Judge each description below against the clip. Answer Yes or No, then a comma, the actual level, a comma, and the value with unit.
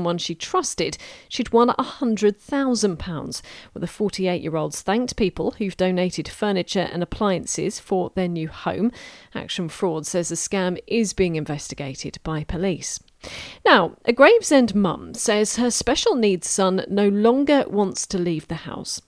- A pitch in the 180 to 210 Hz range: Yes, high, 190 Hz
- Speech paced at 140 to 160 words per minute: Yes, average, 150 wpm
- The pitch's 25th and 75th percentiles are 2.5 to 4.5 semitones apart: No, average, 4.9 semitones